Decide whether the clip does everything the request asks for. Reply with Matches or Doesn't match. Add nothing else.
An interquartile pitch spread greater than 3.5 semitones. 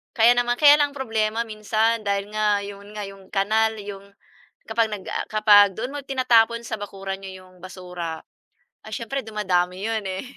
Doesn't match